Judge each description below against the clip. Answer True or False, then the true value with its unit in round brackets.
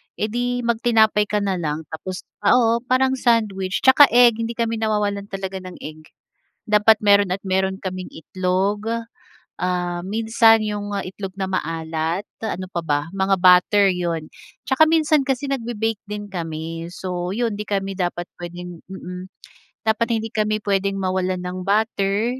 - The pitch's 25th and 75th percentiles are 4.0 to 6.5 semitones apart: False (3.5 semitones)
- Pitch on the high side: True (200 Hz)